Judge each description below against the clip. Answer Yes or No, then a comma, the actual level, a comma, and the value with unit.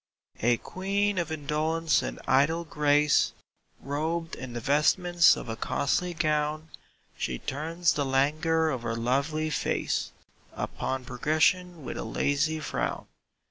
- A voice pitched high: No, medium, 150 Hz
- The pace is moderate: No, slow, 130 wpm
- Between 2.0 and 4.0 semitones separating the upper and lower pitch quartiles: Yes, average, 3.0 semitones